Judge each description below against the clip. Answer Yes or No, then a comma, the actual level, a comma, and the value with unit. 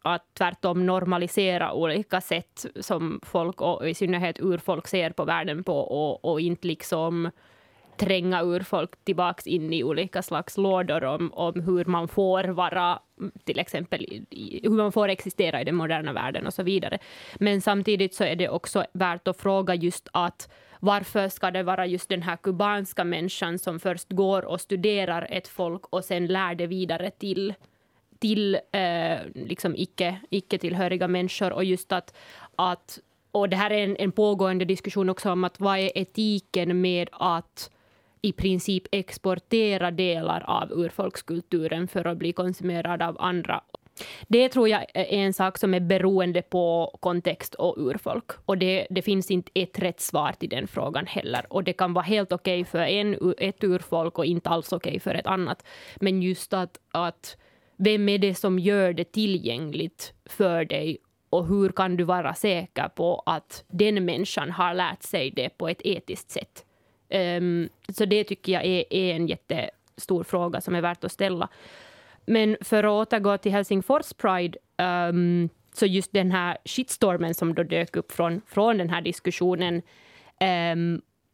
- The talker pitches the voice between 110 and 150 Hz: No, medium, 185 Hz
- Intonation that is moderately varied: No, narrow, 2.1 semitones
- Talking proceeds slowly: No, average, 170 wpm